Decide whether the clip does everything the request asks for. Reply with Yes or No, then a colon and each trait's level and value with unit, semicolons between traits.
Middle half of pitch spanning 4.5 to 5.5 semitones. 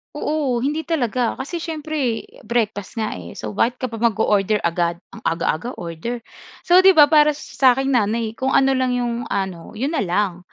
Yes: average, 5.1 semitones